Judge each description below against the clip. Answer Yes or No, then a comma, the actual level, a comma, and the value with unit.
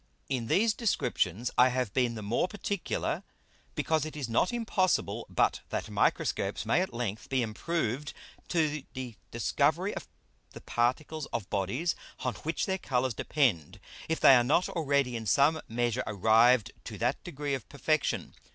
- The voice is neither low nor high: No, low, 130 Hz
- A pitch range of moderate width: Yes, average, 5.0 semitones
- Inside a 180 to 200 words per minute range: No, average, 160 wpm